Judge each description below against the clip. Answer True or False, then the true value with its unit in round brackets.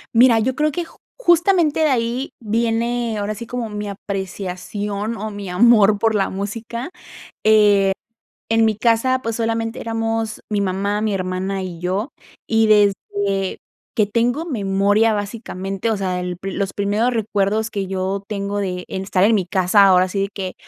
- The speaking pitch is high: True (210 Hz)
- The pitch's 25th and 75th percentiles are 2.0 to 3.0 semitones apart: True (2.7 semitones)